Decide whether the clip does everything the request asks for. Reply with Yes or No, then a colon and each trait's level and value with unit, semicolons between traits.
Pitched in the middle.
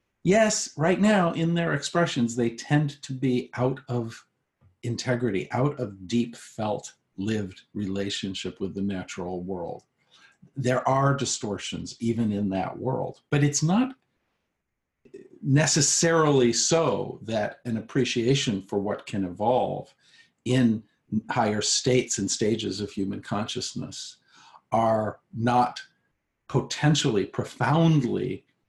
No: low, 120 Hz